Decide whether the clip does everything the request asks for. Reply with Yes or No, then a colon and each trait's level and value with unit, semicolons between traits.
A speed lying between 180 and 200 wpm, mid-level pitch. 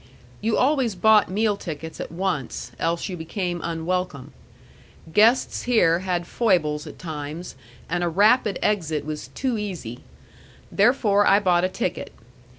No: average, 140 wpm; medium, 180 Hz